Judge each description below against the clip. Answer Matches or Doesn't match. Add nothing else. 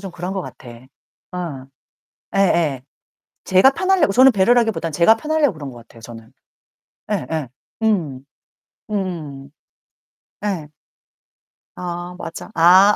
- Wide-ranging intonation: Matches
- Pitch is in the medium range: Matches